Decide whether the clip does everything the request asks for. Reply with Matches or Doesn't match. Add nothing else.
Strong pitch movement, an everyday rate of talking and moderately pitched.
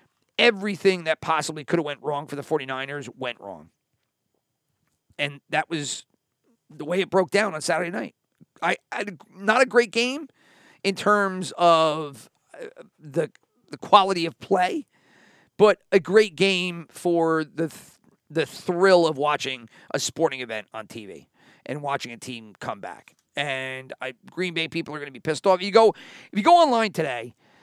Matches